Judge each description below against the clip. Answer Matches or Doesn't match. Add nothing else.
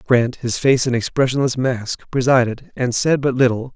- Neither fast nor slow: Matches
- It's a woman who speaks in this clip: Doesn't match